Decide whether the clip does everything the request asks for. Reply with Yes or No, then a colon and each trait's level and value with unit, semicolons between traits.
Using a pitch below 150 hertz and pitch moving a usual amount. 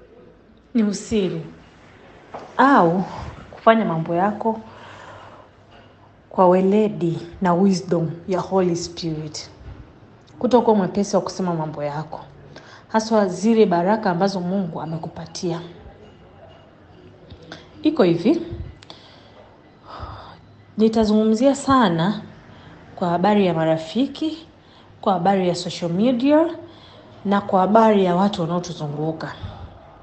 No: medium, 185 Hz; average, 4.6 semitones